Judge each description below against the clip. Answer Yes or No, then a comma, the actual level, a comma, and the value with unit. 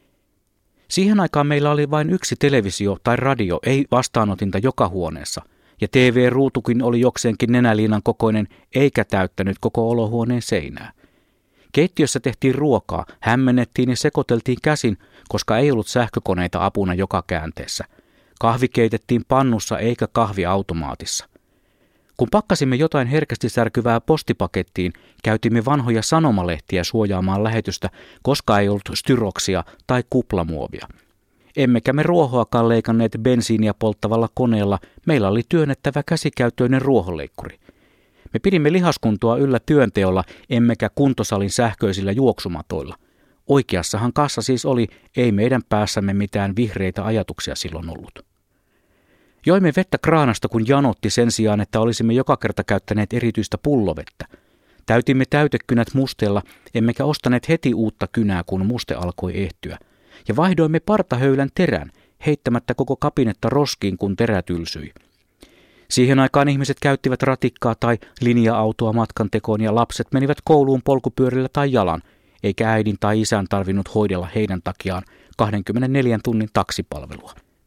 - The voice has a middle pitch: No, low, 115 Hz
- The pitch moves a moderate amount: Yes, average, 4.6 semitones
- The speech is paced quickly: No, average, 120 wpm